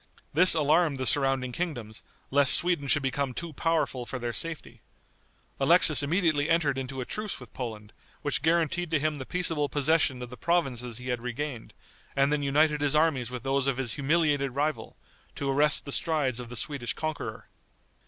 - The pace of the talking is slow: No, average, 180 wpm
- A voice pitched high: No, medium, 140 Hz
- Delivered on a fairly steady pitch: No, average, 3.6 semitones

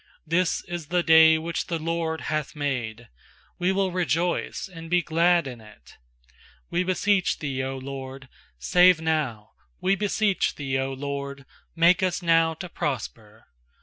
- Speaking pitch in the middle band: Yes, medium, 160 Hz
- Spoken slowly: No, average, 150 wpm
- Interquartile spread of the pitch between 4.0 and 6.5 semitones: Yes, average, 4.5 semitones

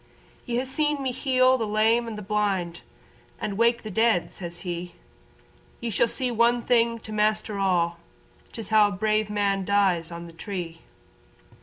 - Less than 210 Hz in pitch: No, high, 215 Hz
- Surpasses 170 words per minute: No, average, 165 wpm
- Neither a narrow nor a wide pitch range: Yes, average, 3.8 semitones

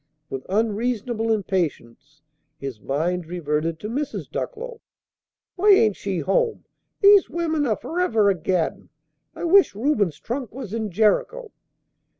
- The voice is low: No, high, 215 Hz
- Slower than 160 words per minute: Yes, slow, 135 wpm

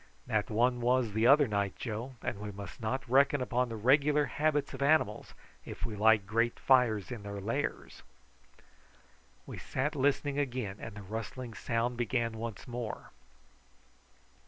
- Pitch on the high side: No, low, 120 Hz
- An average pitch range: Yes, average, 3.4 semitones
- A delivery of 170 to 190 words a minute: No, average, 155 wpm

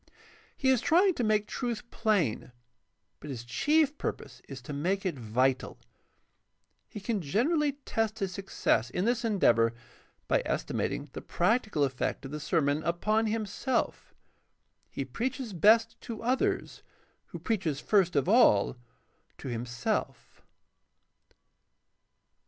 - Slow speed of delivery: Yes, slow, 130 wpm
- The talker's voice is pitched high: Yes, high, 200 Hz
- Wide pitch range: Yes, wide, 8.4 semitones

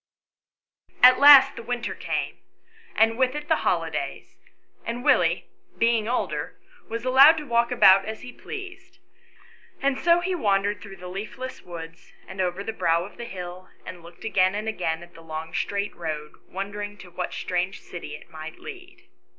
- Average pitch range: No, wide, 6.3 semitones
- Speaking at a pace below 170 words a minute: No, average, 175 wpm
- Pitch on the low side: No, high, 205 Hz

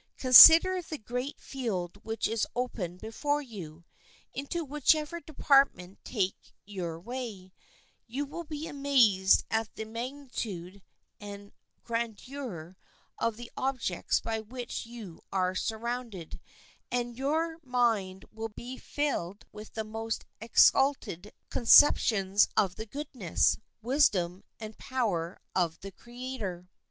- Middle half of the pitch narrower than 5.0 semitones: No, wide, 5.4 semitones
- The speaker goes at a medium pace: No, slow, 120 wpm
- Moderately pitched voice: No, high, 225 Hz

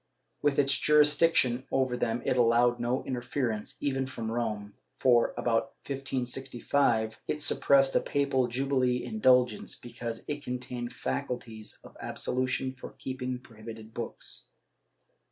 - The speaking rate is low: Yes, slow, 120 wpm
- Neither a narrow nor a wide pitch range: No, narrow, 2.3 semitones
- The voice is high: No, low, 125 Hz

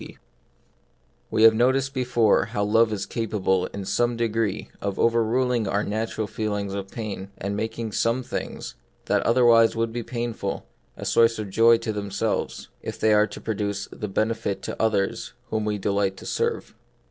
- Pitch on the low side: Yes, low, 110 Hz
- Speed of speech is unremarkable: Yes, average, 175 wpm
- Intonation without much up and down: Yes, narrow, 2.2 semitones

